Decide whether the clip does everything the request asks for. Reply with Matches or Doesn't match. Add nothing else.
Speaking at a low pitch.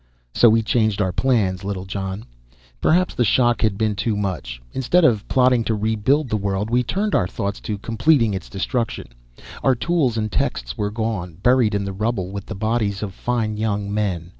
Matches